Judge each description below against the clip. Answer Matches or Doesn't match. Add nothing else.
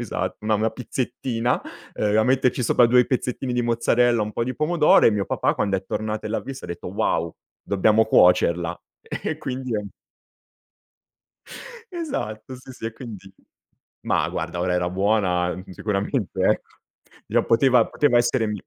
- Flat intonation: Doesn't match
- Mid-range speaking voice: Doesn't match